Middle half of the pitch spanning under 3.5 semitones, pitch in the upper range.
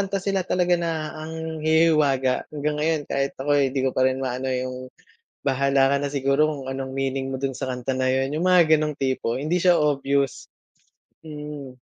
No: average, 2.8 semitones; medium, 140 Hz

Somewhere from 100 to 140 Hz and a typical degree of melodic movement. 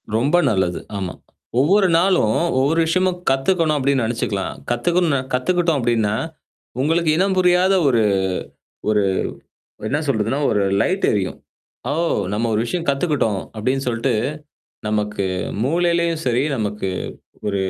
No: low, 135 Hz; wide, 7.7 semitones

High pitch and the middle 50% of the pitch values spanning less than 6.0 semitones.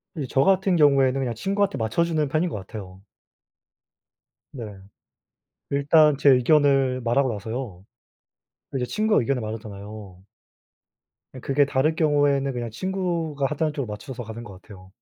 No: low, 135 Hz; wide, 5.4 semitones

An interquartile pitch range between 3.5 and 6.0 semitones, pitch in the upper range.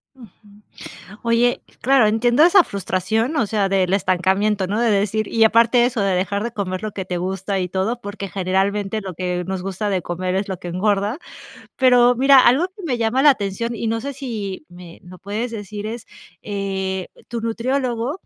Yes: average, 3.8 semitones; high, 210 Hz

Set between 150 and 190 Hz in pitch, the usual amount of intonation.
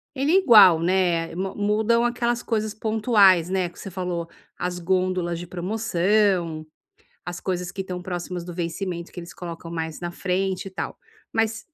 Yes: medium, 185 Hz; average, 3.3 semitones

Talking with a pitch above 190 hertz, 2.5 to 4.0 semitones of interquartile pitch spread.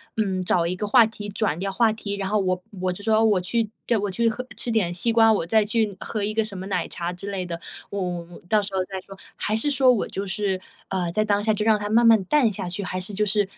Yes: high, 205 Hz; average, 2.9 semitones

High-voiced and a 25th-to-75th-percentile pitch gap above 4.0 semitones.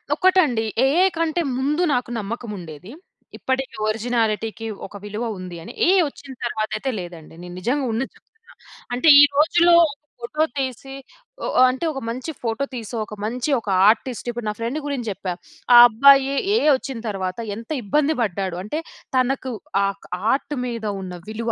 Yes: high, 240 Hz; average, 4.5 semitones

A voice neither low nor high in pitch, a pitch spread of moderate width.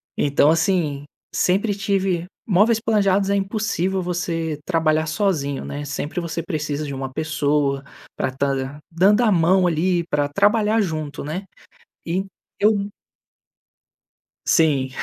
Yes: medium, 165 Hz; average, 4.9 semitones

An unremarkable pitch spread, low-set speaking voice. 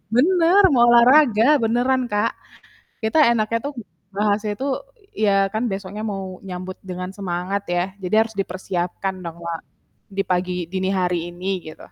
No: average, 3.7 semitones; high, 195 Hz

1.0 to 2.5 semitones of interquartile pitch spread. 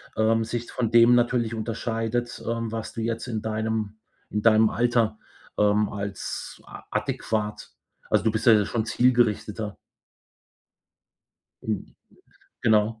Yes: narrow, 1.4 semitones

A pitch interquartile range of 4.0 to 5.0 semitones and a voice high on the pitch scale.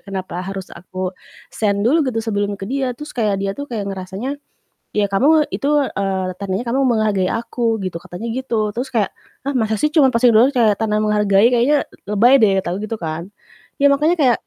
Yes: average, 4.6 semitones; high, 220 Hz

